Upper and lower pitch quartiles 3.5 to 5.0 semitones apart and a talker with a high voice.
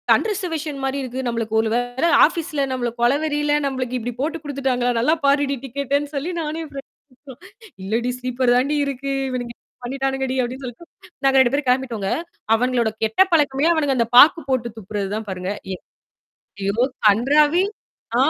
No: average, 3.1 semitones; very high, 265 Hz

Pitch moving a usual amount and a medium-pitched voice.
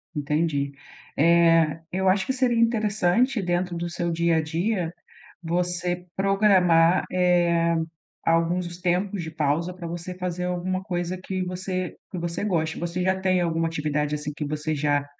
No: narrow, 2.0 semitones; medium, 175 Hz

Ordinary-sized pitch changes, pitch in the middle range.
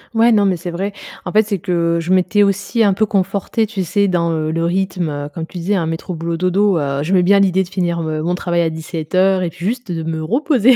Yes: average, 3.1 semitones; medium, 180 Hz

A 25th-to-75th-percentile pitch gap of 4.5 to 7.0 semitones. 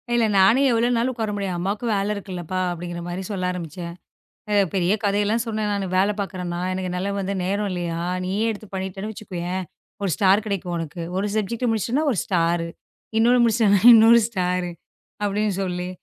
No: average, 3.1 semitones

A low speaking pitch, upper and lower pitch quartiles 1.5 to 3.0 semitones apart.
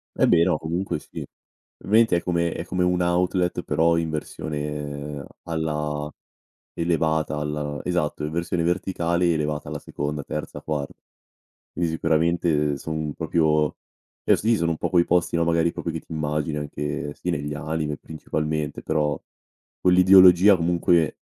Yes: very low, 80 Hz; narrow, 2.4 semitones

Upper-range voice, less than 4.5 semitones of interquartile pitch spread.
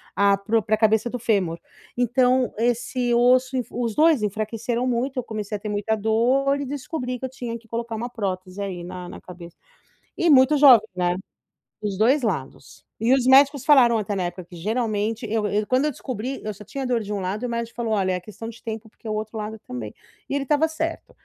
Yes: high, 225 Hz; average, 3.4 semitones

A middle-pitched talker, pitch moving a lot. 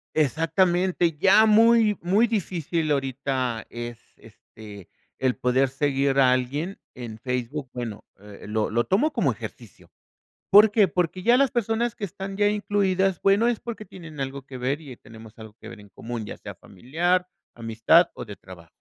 Yes: medium, 145 Hz; wide, 8.3 semitones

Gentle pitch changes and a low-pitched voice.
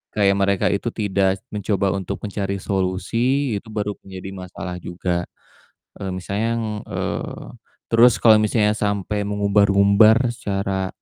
Yes: narrow, 1.9 semitones; low, 100 Hz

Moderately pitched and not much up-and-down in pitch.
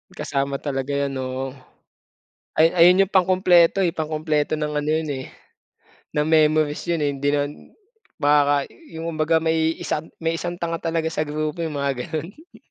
Yes: medium, 155 Hz; narrow, 2.3 semitones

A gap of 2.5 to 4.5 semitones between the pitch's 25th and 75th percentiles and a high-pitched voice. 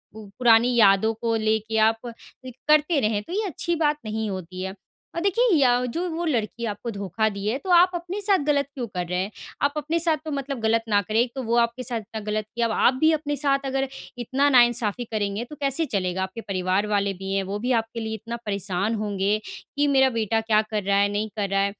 No: average, 5.2 semitones; high, 225 Hz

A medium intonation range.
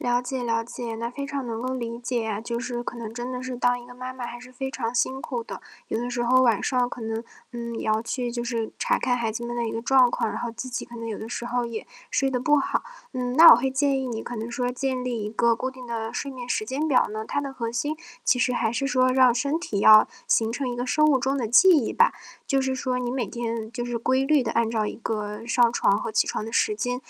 No: narrow, 2.0 semitones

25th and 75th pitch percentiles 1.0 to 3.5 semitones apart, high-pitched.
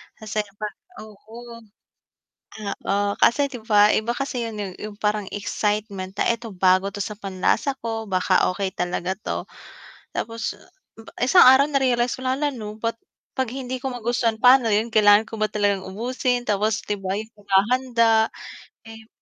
Yes: average, 2.9 semitones; high, 220 Hz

